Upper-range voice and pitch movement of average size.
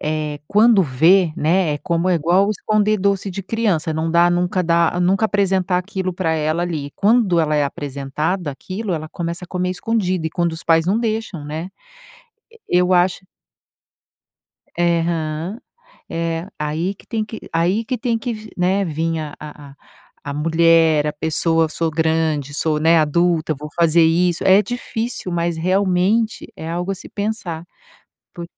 No: medium, 170 Hz; average, 3.1 semitones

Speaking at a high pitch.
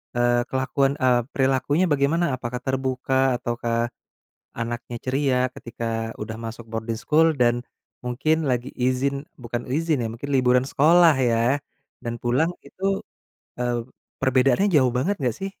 No: low, 130 Hz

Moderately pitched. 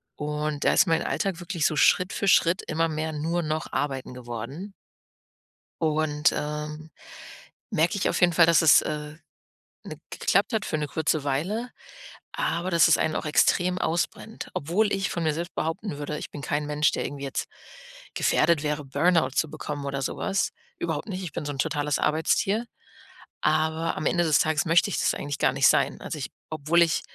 Yes: medium, 155 Hz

